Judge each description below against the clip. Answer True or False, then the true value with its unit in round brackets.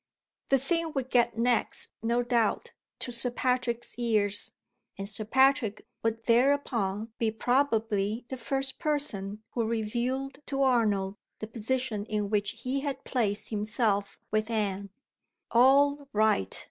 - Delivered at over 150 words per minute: False (135 wpm)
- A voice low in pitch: False (230 Hz)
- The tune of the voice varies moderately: True (3.5 semitones)